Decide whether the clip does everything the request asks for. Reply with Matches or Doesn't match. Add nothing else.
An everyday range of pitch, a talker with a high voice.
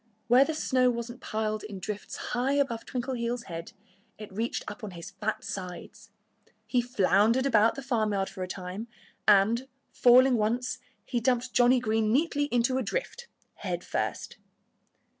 Matches